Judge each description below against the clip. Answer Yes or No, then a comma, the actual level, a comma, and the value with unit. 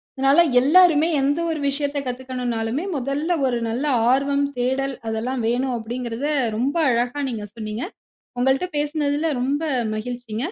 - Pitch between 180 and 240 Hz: No, very high, 265 Hz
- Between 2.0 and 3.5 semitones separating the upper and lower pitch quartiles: Yes, average, 3.0 semitones